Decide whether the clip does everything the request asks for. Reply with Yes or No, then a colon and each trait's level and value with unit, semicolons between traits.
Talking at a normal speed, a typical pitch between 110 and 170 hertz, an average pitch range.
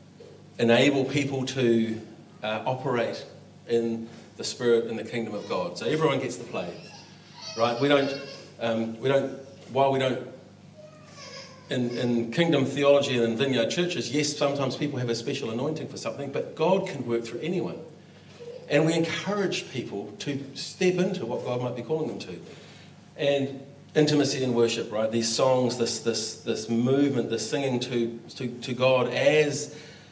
Yes: average, 165 wpm; low, 135 Hz; average, 4.1 semitones